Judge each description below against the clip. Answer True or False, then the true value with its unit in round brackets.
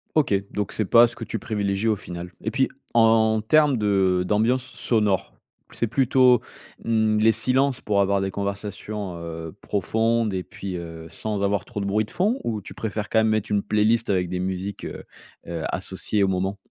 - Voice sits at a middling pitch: False (105 Hz)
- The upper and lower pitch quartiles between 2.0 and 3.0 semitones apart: True (2.7 semitones)